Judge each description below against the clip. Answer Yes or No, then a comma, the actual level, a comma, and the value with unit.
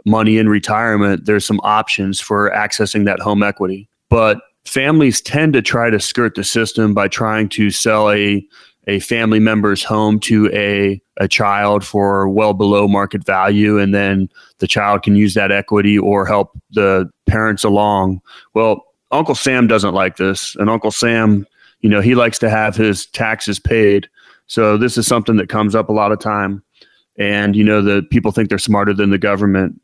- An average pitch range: No, narrow, 1.5 semitones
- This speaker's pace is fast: No, average, 185 wpm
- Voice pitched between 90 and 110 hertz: Yes, low, 105 Hz